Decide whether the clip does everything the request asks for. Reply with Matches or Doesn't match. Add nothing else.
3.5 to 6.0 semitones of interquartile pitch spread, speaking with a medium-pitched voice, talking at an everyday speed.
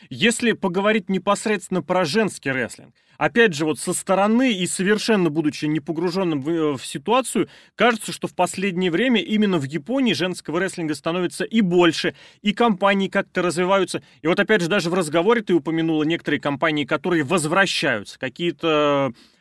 Matches